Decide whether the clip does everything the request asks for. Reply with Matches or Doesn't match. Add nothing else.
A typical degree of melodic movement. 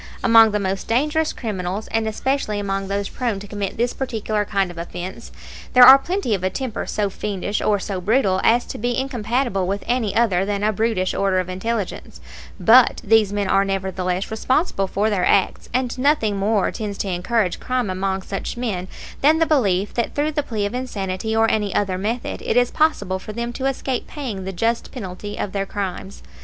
Matches